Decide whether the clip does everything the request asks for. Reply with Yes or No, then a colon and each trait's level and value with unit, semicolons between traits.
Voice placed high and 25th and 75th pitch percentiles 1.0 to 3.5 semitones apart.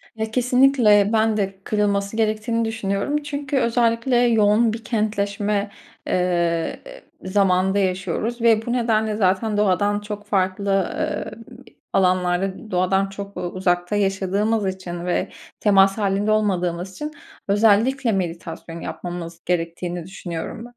Yes: high, 200 Hz; average, 3.1 semitones